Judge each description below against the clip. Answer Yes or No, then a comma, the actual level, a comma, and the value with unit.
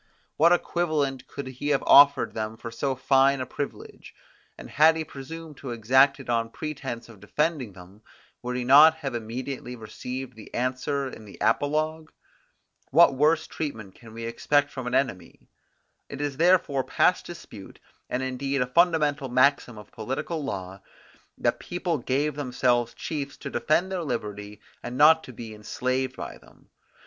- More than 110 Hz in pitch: Yes, low, 135 Hz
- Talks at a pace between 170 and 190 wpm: No, average, 160 wpm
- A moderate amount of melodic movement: Yes, average, 3.8 semitones